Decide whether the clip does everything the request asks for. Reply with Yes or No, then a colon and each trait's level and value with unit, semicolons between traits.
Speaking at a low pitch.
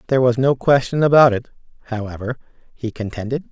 Yes: low, 125 Hz